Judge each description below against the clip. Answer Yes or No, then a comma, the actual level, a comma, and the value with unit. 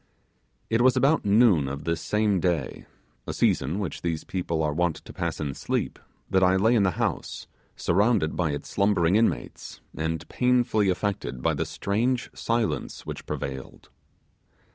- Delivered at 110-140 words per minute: No, average, 160 wpm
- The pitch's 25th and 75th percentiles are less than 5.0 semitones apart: No, average, 5.3 semitones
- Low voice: Yes, very low, 95 Hz